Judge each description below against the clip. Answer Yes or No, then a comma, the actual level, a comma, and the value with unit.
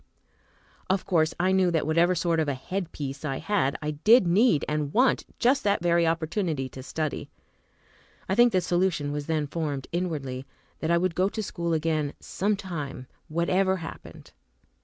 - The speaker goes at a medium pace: Yes, average, 175 wpm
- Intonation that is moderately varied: Yes, average, 3.8 semitones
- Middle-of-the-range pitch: Yes, medium, 170 Hz